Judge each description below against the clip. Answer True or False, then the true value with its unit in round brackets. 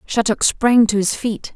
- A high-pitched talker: True (220 Hz)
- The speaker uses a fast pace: False (195 wpm)